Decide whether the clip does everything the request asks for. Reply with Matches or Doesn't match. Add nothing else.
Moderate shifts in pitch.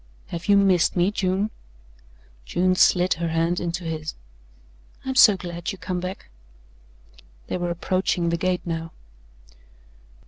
Doesn't match